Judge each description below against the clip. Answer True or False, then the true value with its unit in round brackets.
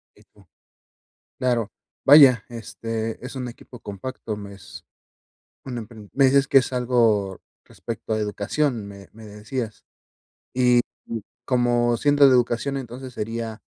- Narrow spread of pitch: False (3.0 semitones)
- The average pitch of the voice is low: True (120 Hz)